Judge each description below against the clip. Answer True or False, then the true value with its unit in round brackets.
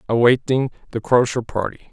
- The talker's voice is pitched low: True (120 Hz)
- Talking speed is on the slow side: True (125 wpm)